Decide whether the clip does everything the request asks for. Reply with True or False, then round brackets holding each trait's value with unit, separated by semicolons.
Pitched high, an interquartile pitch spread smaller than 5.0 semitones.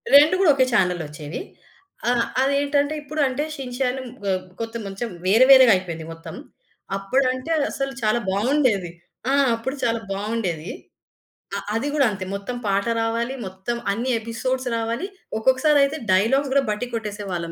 False (230 Hz; 5.3 semitones)